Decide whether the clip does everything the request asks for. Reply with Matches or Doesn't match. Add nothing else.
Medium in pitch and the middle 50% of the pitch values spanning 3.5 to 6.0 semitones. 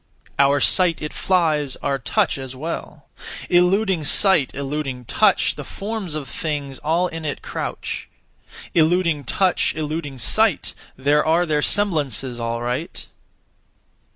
Matches